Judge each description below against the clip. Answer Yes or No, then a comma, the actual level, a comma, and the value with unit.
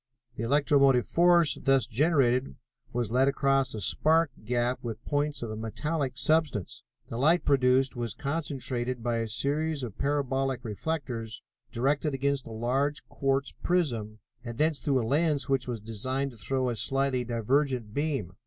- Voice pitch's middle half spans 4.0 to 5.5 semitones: No, average, 3.4 semitones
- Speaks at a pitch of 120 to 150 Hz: Yes, low, 135 Hz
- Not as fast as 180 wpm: Yes, average, 155 wpm